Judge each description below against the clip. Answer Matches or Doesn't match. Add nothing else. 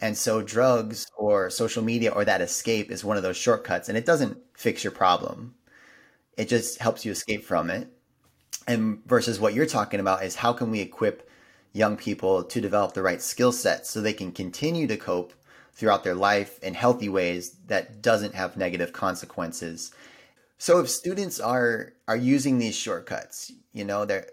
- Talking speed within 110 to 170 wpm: Doesn't match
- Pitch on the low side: Matches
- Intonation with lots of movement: Doesn't match